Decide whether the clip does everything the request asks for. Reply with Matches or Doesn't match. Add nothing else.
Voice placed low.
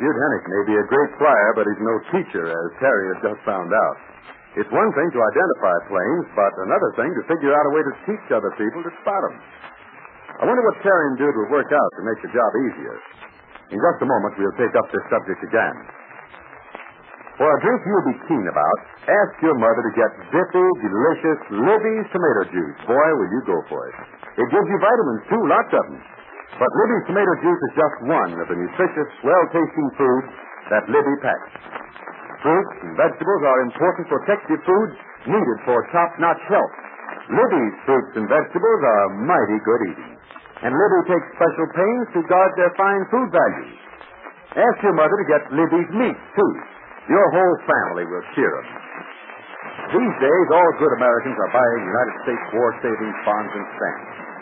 Doesn't match